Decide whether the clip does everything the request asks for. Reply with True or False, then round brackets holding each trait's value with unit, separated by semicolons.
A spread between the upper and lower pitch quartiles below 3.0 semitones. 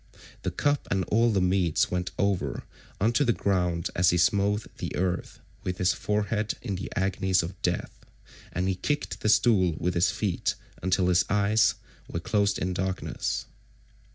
True (2.5 semitones)